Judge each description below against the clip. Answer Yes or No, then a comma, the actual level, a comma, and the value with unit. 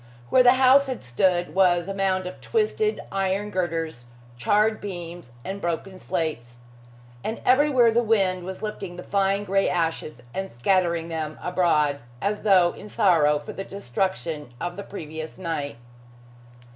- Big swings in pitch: No, average, 3.7 semitones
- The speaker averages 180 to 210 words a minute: No, average, 150 wpm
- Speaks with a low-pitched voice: No, medium, 185 Hz